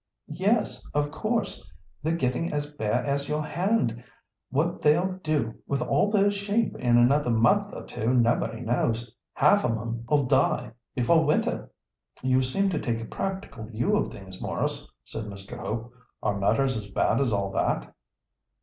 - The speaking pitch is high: No, low, 130 Hz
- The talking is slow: No, average, 160 wpm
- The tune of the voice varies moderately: No, wide, 6.2 semitones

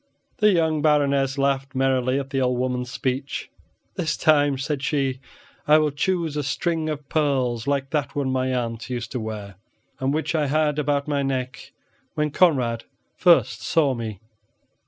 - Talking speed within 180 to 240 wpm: No, average, 165 wpm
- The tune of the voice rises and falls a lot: No, average, 2.7 semitones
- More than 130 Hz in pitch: Yes, medium, 140 Hz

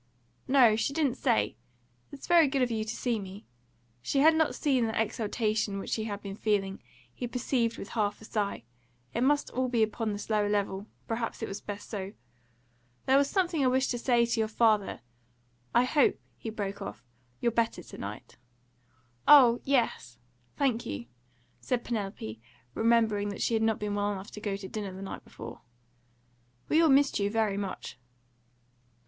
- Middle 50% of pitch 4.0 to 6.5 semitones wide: No, average, 3.6 semitones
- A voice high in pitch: Yes, high, 220 Hz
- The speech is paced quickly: No, average, 180 wpm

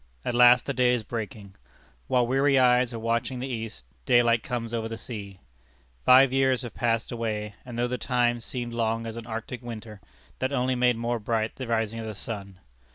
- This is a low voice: Yes, low, 115 Hz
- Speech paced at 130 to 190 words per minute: No, average, 200 wpm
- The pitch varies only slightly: Yes, narrow, 1.8 semitones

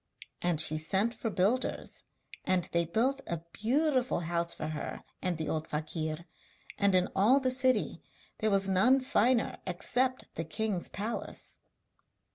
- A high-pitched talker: Yes, high, 195 Hz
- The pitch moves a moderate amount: No, wide, 6.7 semitones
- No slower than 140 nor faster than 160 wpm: Yes, average, 145 wpm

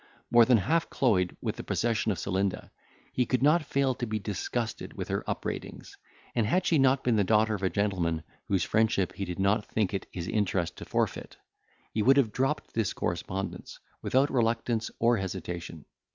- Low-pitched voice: Yes, low, 110 Hz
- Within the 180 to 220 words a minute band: Yes, average, 185 wpm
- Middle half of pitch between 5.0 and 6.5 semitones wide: No, average, 4.5 semitones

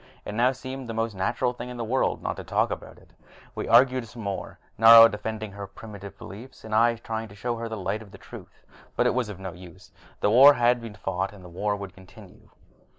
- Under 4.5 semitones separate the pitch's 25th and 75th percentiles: Yes, average, 3.0 semitones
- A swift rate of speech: Yes, fast, 220 wpm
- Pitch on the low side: Yes, low, 110 Hz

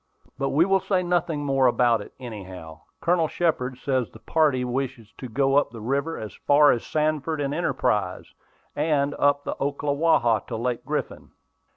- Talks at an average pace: Yes, average, 170 wpm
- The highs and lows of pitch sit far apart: No, average, 4.0 semitones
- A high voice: No, medium, 140 Hz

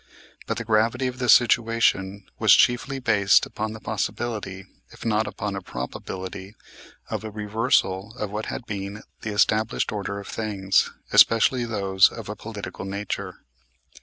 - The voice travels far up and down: No, narrow, 2.6 semitones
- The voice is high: No, low, 105 Hz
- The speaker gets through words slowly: No, average, 150 wpm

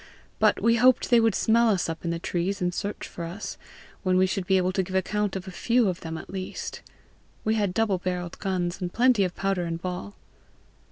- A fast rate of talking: Yes, fast, 225 wpm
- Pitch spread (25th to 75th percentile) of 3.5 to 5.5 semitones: No, average, 2.8 semitones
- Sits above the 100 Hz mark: Yes, high, 190 Hz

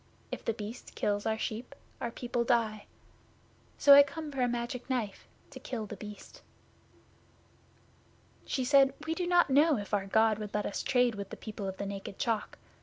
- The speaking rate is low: No, average, 185 wpm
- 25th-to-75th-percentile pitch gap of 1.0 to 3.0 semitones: No, average, 4.1 semitones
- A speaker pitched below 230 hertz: No, high, 235 Hz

